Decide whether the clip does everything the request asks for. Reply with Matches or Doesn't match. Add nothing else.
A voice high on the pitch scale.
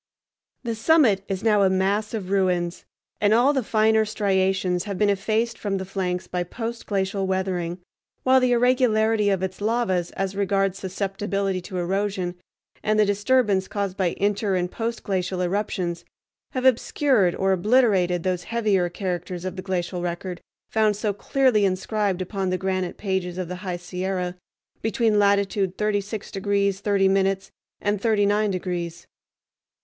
Matches